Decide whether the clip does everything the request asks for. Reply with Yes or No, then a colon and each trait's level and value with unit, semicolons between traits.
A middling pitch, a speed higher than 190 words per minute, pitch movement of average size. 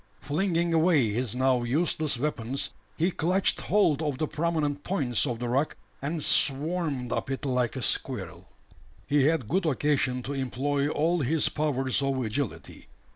No: medium, 145 Hz; average, 155 wpm; average, 3.7 semitones